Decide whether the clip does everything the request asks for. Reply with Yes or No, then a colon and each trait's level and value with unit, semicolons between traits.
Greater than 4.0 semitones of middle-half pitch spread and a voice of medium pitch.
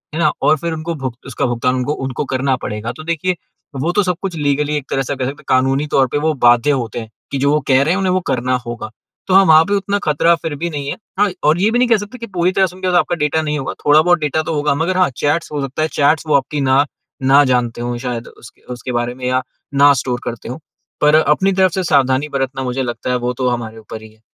Yes: average, 4.6 semitones; medium, 145 Hz